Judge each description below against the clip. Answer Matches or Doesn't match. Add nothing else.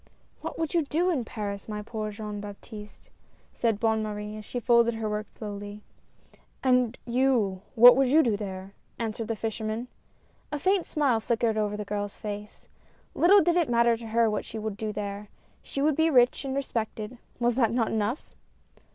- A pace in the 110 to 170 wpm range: Doesn't match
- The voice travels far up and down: Doesn't match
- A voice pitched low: Doesn't match